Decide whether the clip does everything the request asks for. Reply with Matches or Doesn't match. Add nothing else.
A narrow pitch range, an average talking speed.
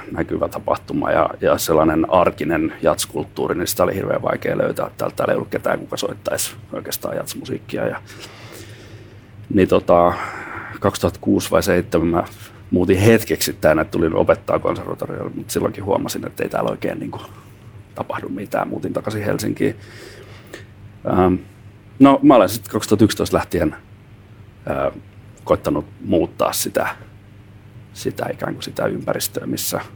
Matches